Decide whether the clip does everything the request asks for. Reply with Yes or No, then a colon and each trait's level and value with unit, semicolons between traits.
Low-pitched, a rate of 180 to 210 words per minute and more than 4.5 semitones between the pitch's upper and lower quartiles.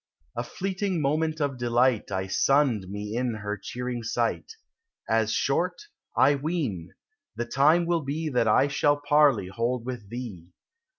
No: low, 125 Hz; average, 145 wpm; average, 5.1 semitones